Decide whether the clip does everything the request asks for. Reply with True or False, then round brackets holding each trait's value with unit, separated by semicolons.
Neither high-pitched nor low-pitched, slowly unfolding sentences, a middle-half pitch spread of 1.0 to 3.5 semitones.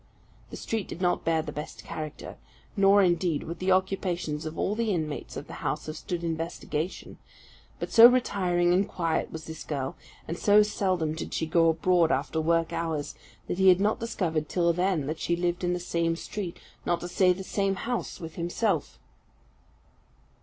False (175 Hz; 185 wpm; 2.8 semitones)